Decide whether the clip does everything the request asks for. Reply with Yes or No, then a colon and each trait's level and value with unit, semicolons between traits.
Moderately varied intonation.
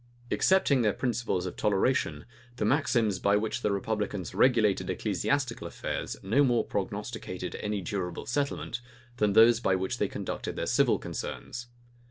Yes: average, 3.8 semitones